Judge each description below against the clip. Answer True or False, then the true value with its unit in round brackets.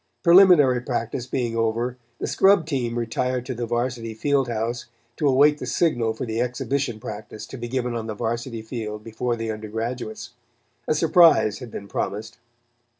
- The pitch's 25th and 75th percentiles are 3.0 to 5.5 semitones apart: False (2.6 semitones)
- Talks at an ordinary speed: True (165 wpm)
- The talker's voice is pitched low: True (120 Hz)